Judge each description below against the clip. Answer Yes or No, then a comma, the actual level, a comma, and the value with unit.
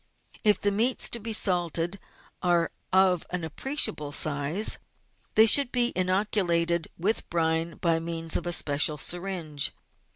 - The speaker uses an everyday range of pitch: Yes, average, 3.8 semitones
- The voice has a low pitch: No, medium, 175 Hz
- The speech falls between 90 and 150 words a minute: Yes, slow, 135 wpm